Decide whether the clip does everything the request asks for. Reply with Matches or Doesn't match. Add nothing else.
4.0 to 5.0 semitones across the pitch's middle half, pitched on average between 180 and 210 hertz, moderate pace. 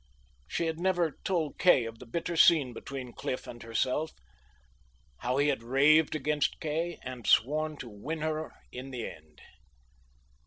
Doesn't match